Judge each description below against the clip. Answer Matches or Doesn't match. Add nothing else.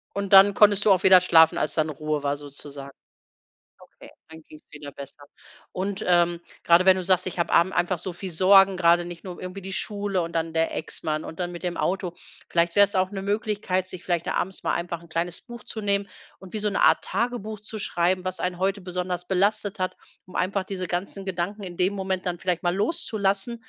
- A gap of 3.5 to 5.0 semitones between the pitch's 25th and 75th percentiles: Doesn't match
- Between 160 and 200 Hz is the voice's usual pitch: Matches